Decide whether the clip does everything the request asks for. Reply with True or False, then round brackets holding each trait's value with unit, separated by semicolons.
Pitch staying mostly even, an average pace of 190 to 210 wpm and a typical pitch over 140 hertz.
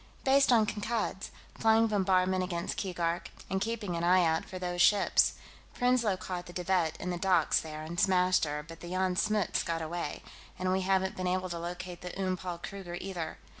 True (1.8 semitones; 200 wpm; 185 Hz)